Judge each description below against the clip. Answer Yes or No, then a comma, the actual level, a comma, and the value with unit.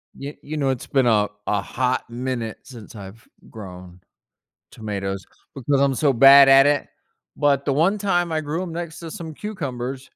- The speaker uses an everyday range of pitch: Yes, average, 5.0 semitones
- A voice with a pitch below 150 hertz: Yes, low, 135 Hz